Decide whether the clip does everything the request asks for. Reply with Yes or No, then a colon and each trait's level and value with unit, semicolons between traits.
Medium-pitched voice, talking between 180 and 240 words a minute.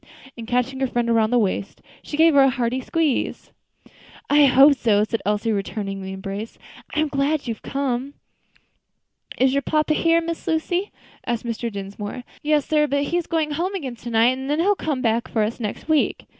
No: very high, 260 Hz; average, 200 wpm